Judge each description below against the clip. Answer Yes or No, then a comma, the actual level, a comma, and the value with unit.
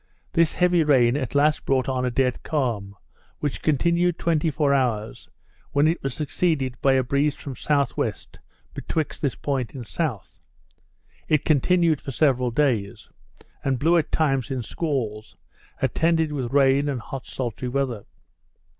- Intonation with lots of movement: No, average, 3.4 semitones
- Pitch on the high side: No, medium, 140 Hz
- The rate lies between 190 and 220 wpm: No, average, 150 wpm